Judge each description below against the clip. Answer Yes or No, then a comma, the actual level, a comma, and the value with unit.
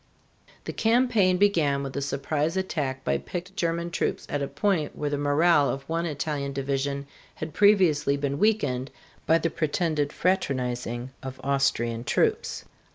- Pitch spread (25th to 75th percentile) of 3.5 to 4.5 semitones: Yes, average, 3.9 semitones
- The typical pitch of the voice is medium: Yes, medium, 145 Hz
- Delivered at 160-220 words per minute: No, average, 150 wpm